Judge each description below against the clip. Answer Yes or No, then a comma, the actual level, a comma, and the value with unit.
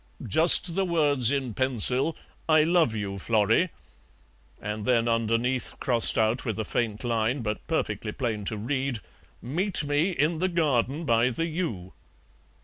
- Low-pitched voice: Yes, low, 125 Hz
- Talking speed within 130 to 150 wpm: Yes, average, 145 wpm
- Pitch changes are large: Yes, wide, 5.9 semitones